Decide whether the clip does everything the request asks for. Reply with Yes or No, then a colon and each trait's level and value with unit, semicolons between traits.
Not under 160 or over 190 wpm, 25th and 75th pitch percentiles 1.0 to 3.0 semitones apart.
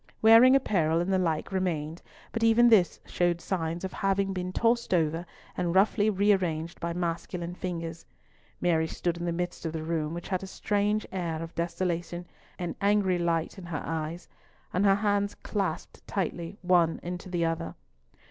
Yes: average, 170 wpm; average, 2.7 semitones